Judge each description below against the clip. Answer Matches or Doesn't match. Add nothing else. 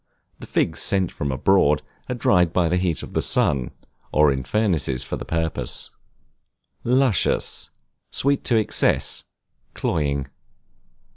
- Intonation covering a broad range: Matches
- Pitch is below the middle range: Matches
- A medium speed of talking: Doesn't match